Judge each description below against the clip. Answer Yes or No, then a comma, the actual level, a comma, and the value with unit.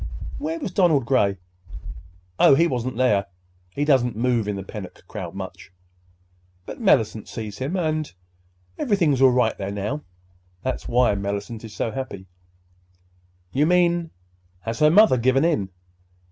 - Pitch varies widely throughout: Yes, wide, 6.9 semitones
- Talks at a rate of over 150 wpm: No, average, 140 wpm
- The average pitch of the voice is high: No, low, 125 Hz